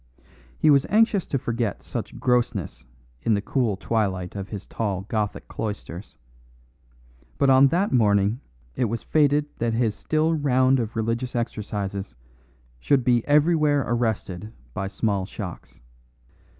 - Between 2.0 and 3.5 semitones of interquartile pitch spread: No, average, 5.0 semitones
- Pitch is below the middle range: Yes, low, 115 Hz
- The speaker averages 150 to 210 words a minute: No, slow, 135 wpm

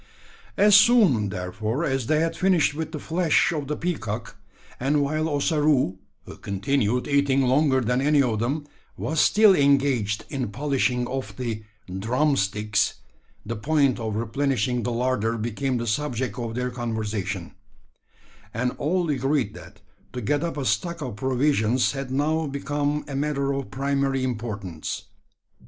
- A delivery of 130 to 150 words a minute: Yes, average, 145 wpm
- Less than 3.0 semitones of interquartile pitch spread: No, average, 4.2 semitones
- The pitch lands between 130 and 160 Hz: Yes, low, 135 Hz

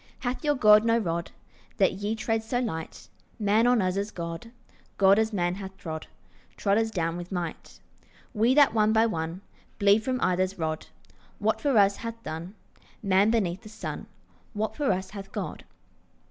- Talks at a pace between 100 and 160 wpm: No, average, 175 wpm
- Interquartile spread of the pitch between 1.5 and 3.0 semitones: No, average, 3.6 semitones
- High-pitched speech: Yes, high, 205 Hz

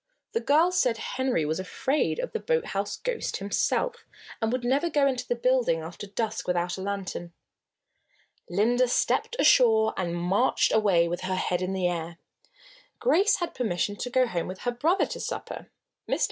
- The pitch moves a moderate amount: No, wide, 6.6 semitones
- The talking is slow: No, average, 175 wpm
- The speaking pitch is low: No, high, 225 Hz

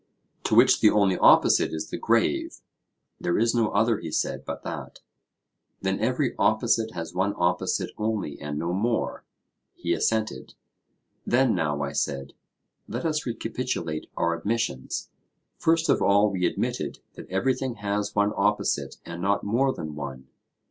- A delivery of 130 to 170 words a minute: Yes, average, 150 wpm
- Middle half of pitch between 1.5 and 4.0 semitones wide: No, average, 5.3 semitones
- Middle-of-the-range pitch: No, low, 100 Hz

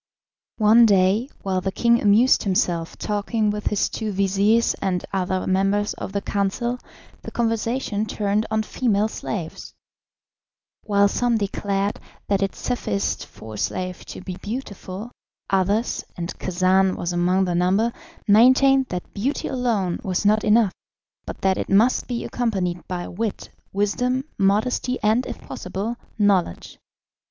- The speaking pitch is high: Yes, high, 205 Hz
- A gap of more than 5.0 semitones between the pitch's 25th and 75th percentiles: No, average, 3.3 semitones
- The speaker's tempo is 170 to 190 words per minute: No, average, 140 wpm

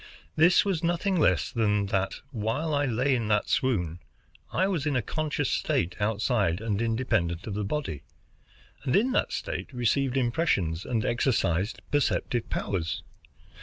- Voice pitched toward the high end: No, low, 120 Hz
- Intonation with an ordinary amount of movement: No, wide, 6.3 semitones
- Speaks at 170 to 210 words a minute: No, average, 150 wpm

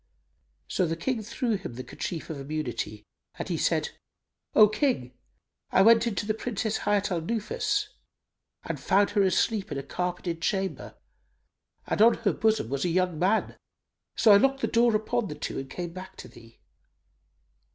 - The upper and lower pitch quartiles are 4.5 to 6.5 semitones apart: Yes, average, 5.0 semitones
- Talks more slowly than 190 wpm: Yes, average, 170 wpm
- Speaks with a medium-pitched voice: No, high, 195 Hz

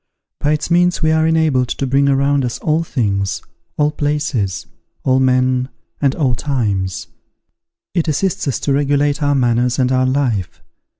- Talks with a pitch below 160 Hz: Yes, medium, 140 Hz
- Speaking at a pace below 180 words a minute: Yes, average, 160 wpm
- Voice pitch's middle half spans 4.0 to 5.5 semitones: No, average, 2.9 semitones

